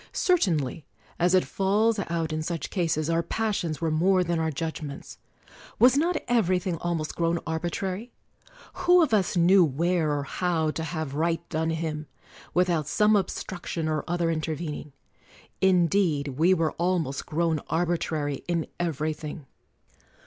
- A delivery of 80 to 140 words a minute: No, average, 150 wpm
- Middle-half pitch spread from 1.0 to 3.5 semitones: Yes, average, 2.7 semitones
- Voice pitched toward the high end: No, medium, 170 Hz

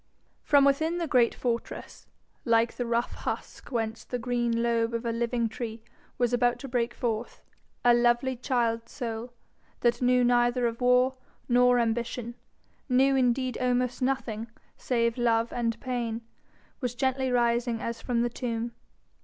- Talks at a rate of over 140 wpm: Yes, average, 150 wpm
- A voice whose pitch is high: Yes, high, 240 Hz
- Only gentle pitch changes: Yes, narrow, 1.3 semitones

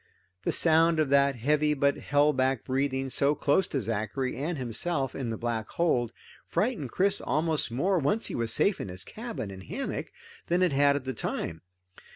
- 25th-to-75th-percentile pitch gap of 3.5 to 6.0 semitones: Yes, average, 4.5 semitones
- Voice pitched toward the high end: No, medium, 140 Hz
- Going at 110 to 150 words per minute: No, average, 190 wpm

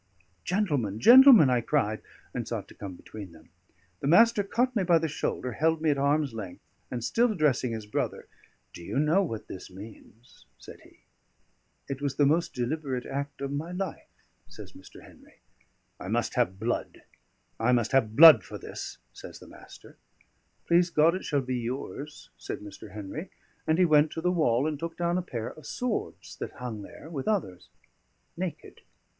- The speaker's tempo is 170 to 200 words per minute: Yes, average, 180 wpm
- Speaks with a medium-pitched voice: Yes, medium, 145 Hz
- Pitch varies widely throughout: Yes, wide, 6.5 semitones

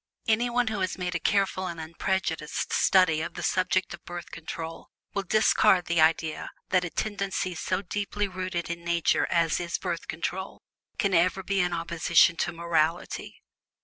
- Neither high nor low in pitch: Yes, medium, 180 Hz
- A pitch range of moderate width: No, narrow, 2.3 semitones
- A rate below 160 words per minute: No, average, 170 wpm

